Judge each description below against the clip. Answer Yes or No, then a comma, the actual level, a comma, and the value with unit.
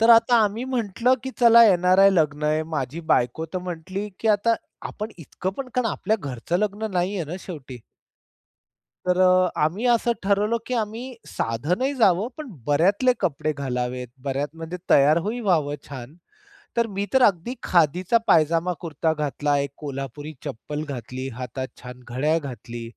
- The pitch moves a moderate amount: No, wide, 6.7 semitones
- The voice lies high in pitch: No, medium, 170 Hz